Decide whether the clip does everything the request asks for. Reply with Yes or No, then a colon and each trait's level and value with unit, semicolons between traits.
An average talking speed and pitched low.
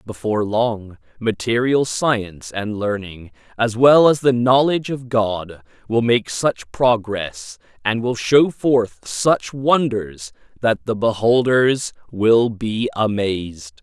No: slow, 125 wpm; low, 115 Hz